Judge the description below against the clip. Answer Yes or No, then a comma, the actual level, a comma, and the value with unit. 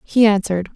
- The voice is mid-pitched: No, high, 205 Hz